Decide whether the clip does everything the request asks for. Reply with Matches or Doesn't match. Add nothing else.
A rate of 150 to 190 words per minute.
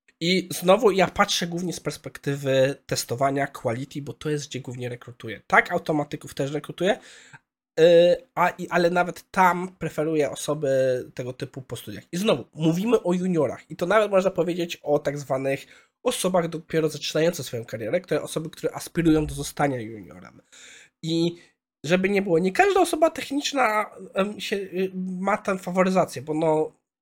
Matches